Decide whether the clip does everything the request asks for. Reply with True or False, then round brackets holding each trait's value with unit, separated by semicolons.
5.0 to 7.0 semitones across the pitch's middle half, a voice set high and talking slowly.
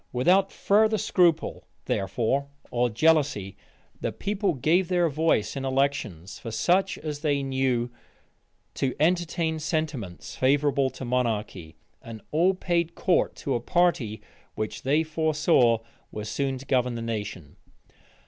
False (5.6 semitones; 140 Hz; 130 wpm)